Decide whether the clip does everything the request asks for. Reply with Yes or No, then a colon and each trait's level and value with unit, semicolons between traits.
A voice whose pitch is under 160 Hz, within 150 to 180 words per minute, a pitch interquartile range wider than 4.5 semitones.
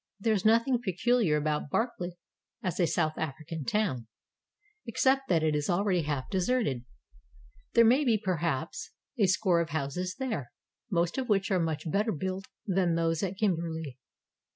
No: medium, 180 Hz; average, 160 wpm; average, 5.2 semitones